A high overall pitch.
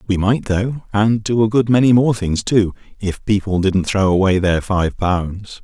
No: low, 100 Hz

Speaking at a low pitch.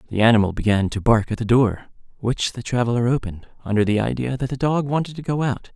Yes: low, 120 Hz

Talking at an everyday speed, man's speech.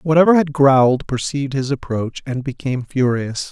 Yes: average, 155 wpm; male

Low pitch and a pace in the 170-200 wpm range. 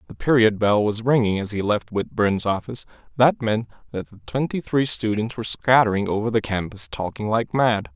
Yes: low, 110 Hz; average, 190 wpm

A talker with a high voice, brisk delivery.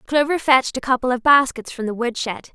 Yes: very high, 260 Hz; fast, 235 wpm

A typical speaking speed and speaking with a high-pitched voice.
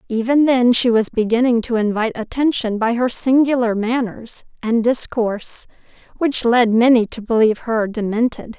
Yes: average, 145 wpm; high, 235 Hz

